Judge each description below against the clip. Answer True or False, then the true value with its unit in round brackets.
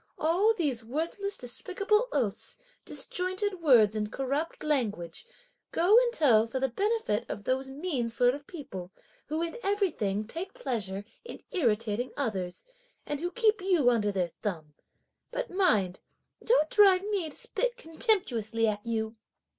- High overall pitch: True (285 Hz)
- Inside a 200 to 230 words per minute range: False (145 wpm)